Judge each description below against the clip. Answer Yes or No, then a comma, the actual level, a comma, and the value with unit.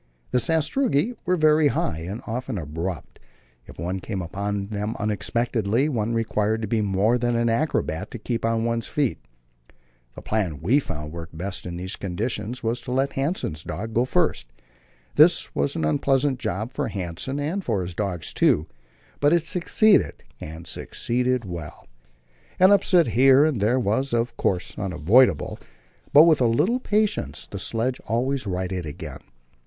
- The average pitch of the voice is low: Yes, low, 115 Hz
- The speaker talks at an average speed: Yes, average, 165 wpm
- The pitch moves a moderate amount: No, wide, 6.1 semitones